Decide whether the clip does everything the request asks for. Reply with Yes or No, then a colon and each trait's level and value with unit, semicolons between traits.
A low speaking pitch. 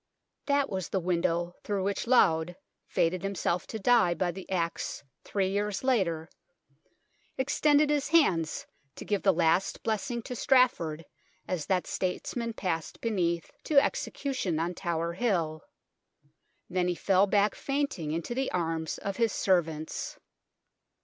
No: high, 190 Hz